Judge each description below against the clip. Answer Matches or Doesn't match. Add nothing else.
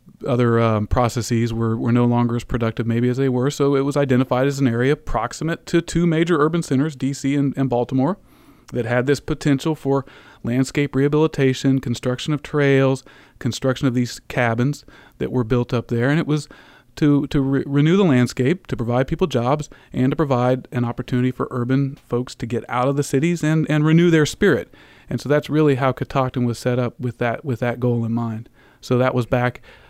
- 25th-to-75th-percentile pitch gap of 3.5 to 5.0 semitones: Doesn't match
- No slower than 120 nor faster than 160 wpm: Doesn't match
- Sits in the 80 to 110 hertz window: Doesn't match